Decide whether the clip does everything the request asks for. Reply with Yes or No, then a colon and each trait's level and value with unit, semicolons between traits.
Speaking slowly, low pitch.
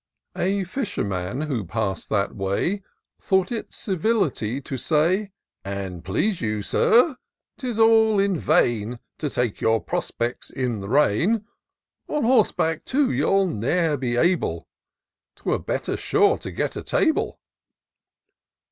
No: slow, 130 wpm; medium, 155 Hz